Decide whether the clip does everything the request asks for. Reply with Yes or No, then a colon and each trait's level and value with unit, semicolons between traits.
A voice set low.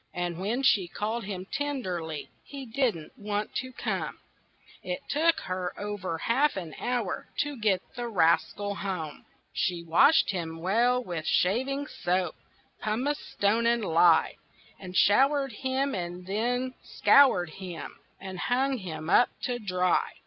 No: high, 205 Hz